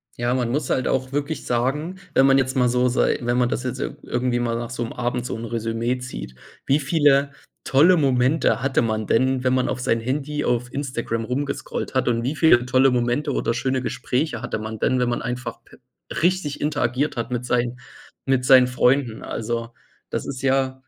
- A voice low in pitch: Yes, low, 125 Hz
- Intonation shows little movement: Yes, narrow, 2.1 semitones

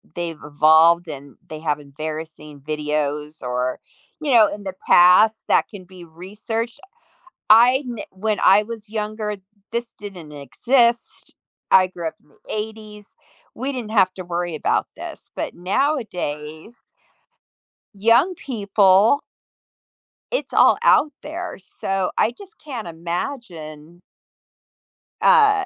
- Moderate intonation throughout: No, wide, 6.4 semitones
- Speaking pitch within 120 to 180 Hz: No, high, 190 Hz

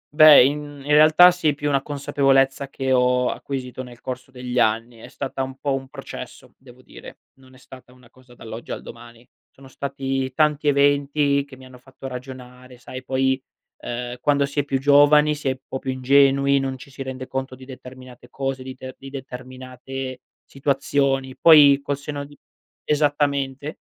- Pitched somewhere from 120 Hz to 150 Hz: Yes, low, 135 Hz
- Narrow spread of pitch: Yes, narrow, 1.6 semitones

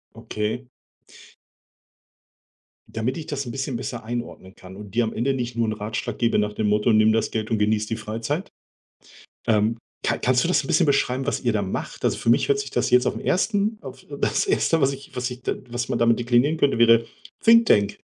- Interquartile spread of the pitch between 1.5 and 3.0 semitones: No, average, 3.8 semitones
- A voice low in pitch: Yes, low, 120 Hz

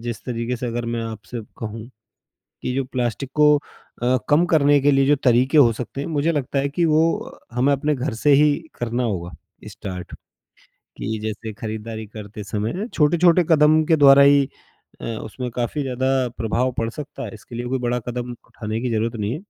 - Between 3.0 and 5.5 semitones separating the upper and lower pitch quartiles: Yes, average, 4.0 semitones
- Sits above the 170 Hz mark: No, low, 125 Hz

